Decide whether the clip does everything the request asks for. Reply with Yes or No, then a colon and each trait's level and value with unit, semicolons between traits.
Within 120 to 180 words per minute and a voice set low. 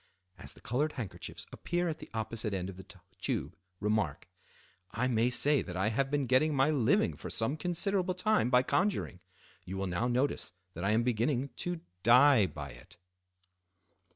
Yes: average, 170 wpm; low, 125 Hz